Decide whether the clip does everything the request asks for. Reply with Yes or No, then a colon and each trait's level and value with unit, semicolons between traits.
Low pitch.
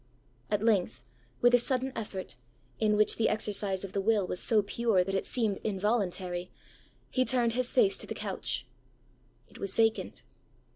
No: high, 215 Hz